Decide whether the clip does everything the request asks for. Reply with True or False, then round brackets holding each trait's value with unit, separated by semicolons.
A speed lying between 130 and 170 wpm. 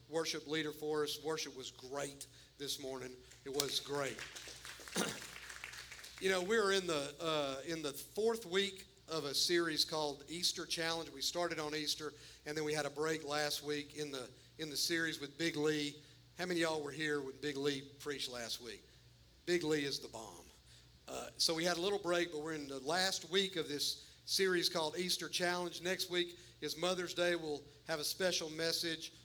False (195 wpm)